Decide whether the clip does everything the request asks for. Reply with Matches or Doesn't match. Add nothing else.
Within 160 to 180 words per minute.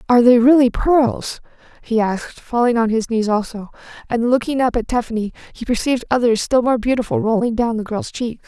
Doesn't match